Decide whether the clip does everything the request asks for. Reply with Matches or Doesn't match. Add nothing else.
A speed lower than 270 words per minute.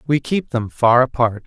Matches